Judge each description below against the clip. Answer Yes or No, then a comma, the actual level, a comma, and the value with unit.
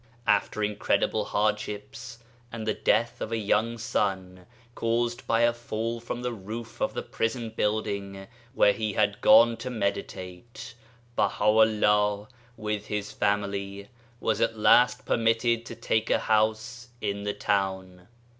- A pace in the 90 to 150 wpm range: Yes, average, 145 wpm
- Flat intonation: Yes, narrow, 2.1 semitones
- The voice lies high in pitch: No, low, 110 Hz